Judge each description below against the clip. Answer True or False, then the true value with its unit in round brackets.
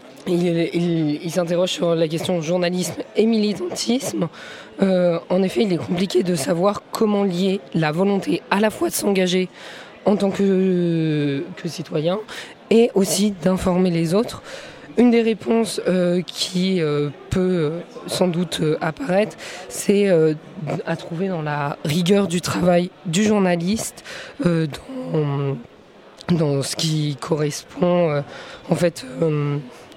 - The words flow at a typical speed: False (135 wpm)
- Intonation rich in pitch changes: False (3.1 semitones)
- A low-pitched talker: False (180 Hz)